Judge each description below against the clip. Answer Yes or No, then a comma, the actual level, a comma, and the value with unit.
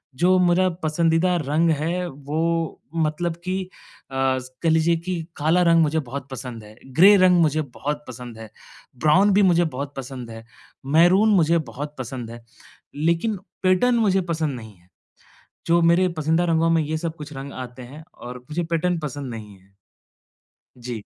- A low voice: No, medium, 155 Hz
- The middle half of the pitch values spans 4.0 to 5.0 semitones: Yes, average, 4.5 semitones